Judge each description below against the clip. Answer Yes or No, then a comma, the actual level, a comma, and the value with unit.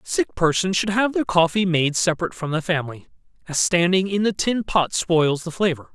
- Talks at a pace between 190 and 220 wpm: Yes, average, 200 wpm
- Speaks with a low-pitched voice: No, medium, 175 Hz